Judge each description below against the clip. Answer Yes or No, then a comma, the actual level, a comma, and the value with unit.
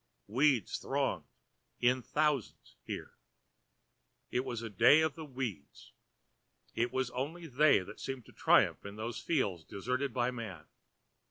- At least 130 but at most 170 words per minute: Yes, average, 140 wpm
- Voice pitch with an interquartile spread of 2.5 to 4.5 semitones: Yes, average, 4.1 semitones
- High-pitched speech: No, low, 125 Hz